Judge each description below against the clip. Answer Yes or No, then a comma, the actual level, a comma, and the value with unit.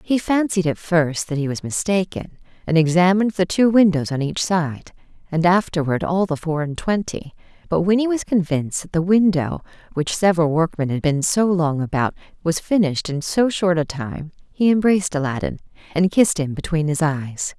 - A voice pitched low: No, medium, 170 Hz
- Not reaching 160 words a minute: No, average, 190 wpm